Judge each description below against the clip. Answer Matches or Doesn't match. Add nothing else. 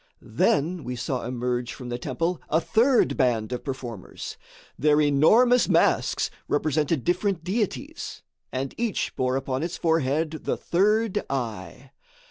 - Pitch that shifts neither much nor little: Doesn't match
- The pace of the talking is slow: Matches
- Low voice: Doesn't match